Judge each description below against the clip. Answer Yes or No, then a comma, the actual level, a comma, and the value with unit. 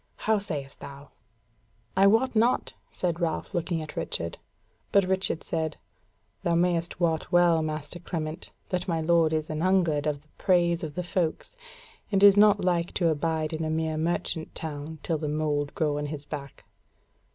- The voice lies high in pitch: No, medium, 165 Hz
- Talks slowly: No, average, 165 wpm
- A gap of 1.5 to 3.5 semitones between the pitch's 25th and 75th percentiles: Yes, narrow, 2.6 semitones